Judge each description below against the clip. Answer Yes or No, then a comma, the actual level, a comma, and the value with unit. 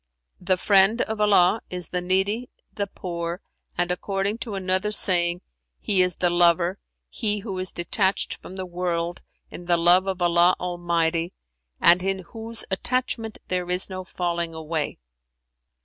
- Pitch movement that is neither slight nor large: No, narrow, 2.0 semitones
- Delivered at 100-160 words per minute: Yes, average, 155 wpm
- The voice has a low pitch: No, medium, 180 Hz